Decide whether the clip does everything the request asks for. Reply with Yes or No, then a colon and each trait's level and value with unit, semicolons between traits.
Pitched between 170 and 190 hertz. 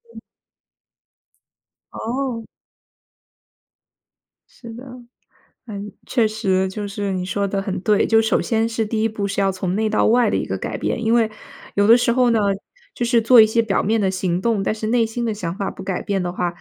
No: high, 215 Hz